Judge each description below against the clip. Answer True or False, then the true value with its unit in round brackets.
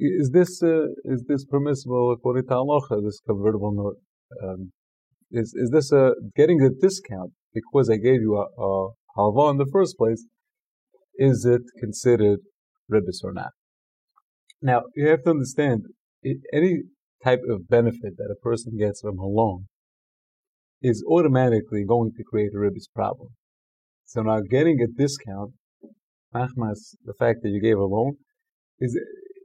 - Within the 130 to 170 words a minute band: True (155 wpm)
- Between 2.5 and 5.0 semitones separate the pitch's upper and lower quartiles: False (5.5 semitones)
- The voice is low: True (120 Hz)